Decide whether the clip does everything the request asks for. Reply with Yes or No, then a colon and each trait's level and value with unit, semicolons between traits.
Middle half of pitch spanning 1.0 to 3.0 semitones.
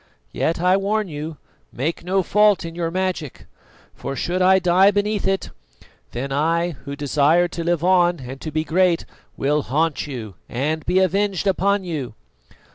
No: average, 4.0 semitones